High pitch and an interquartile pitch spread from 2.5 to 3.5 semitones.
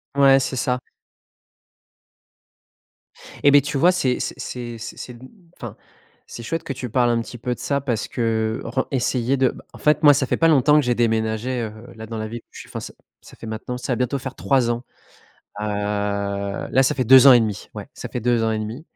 No: low, 120 Hz; average, 3.1 semitones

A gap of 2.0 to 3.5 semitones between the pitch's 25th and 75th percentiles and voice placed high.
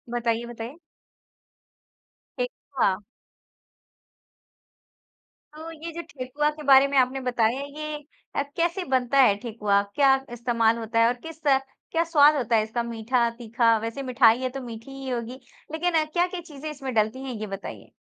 No: average, 4.3 semitones; very high, 255 Hz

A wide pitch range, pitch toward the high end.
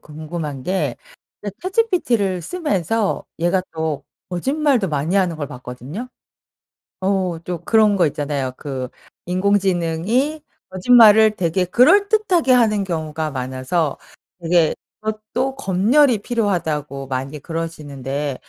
No: wide, 6.5 semitones; medium, 180 Hz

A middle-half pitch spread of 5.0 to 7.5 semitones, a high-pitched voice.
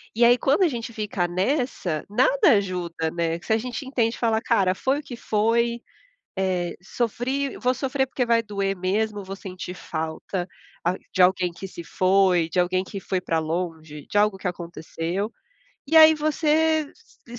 Yes: average, 5.3 semitones; high, 200 Hz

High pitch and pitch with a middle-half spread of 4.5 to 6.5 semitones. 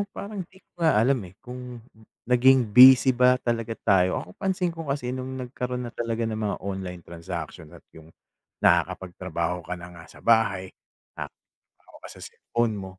No: low, 115 Hz; wide, 5.6 semitones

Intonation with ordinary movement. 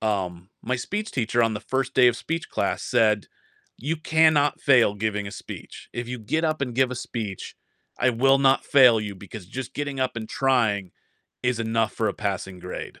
Yes: average, 4.2 semitones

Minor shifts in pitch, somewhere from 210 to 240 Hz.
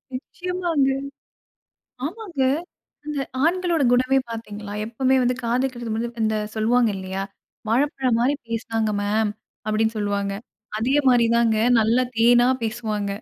No: average, 3.5 semitones; high, 235 Hz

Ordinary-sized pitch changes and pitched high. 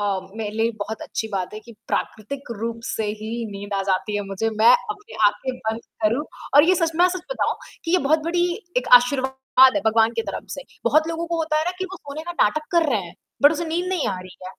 No: wide, 7.1 semitones; very high, 260 Hz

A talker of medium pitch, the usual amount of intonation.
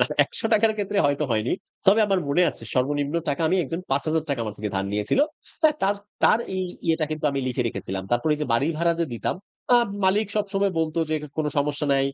No: medium, 155 Hz; wide, 5.7 semitones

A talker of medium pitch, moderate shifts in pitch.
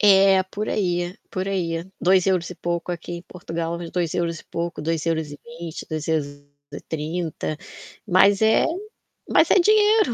Yes: medium, 175 Hz; average, 3.0 semitones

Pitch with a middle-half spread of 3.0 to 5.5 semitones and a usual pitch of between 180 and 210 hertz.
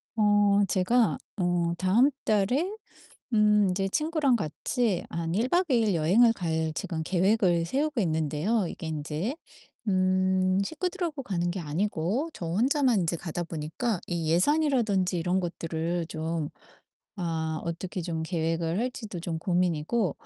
Yes: average, 5.2 semitones; medium, 185 Hz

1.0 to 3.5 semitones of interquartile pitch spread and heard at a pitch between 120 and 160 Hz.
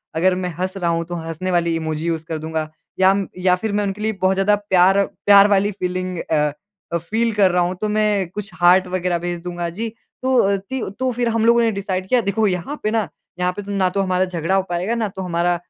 No: average, 2.8 semitones; medium, 185 Hz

